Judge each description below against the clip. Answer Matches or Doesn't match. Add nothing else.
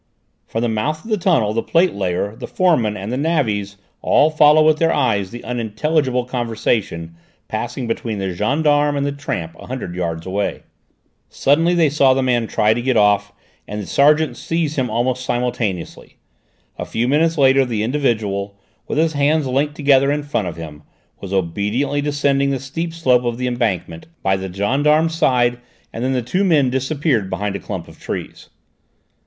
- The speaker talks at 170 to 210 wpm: Matches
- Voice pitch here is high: Doesn't match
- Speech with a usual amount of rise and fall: Doesn't match